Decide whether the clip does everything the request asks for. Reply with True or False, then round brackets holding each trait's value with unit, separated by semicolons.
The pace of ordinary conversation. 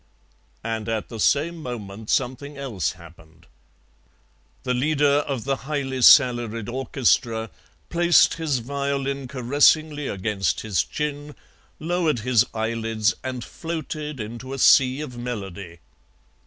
False (115 wpm)